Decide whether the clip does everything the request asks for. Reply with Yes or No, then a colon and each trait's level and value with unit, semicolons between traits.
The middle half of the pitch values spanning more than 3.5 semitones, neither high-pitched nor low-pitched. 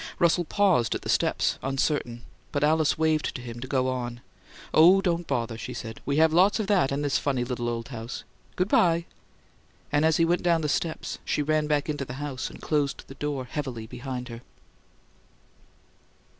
Yes: average, 4.3 semitones; medium, 145 Hz